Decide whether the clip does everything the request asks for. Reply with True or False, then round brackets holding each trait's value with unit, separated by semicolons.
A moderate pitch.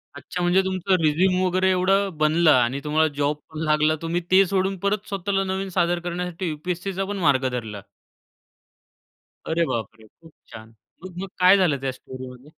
True (175 Hz)